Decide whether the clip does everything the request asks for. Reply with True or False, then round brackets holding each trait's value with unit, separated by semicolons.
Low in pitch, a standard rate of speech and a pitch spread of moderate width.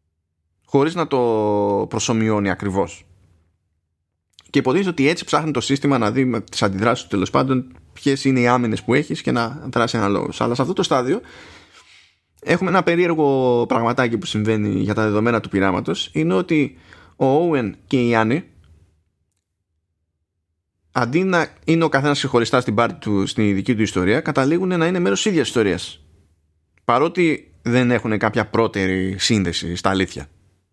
False (110 Hz; 155 wpm; 6.0 semitones)